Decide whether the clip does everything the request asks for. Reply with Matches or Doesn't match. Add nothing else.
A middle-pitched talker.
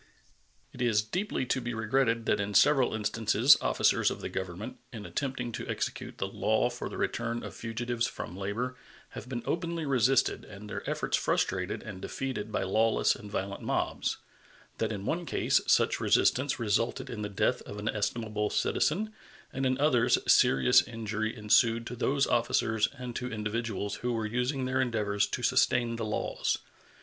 Doesn't match